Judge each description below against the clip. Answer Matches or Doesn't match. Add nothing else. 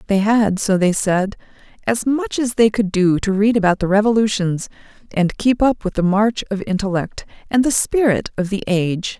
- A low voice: Doesn't match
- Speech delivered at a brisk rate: Doesn't match